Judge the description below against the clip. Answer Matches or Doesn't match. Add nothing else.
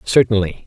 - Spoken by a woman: Doesn't match